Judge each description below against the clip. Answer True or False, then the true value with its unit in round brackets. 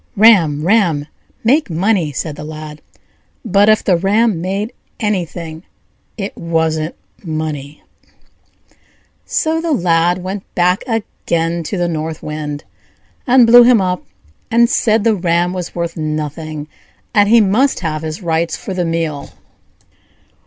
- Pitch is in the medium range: True (175 Hz)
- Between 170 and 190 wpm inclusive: False (135 wpm)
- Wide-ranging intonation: False (4.9 semitones)